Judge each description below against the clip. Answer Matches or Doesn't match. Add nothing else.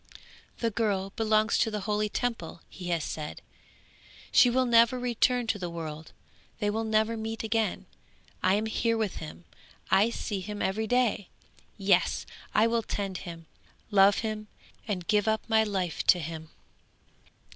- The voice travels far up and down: Doesn't match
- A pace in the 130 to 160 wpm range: Matches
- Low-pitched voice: Doesn't match